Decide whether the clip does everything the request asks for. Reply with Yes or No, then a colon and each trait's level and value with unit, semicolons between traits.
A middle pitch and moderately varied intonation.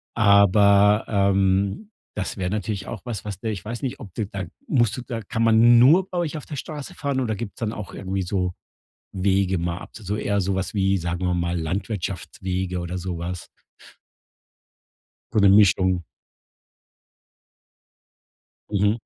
No: low, 100 Hz; average, 3.2 semitones